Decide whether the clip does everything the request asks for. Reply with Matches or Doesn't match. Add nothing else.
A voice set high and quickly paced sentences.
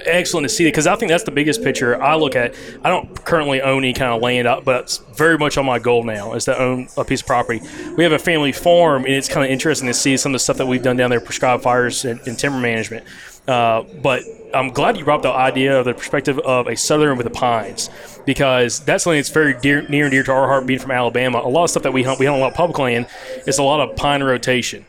Doesn't match